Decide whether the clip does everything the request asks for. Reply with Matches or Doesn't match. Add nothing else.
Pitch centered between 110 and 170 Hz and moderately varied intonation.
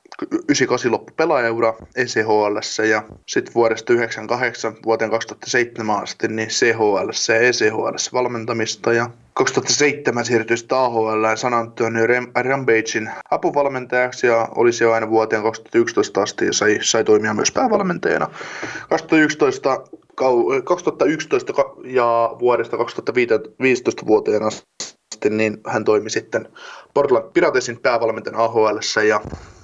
Matches